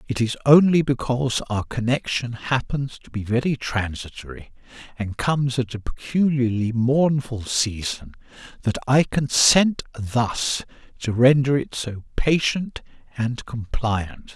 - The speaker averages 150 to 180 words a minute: No, slow, 135 wpm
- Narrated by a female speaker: No, male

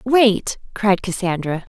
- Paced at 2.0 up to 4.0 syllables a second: Yes, 3.5 syllables/s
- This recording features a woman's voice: Yes, female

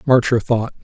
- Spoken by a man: Yes, male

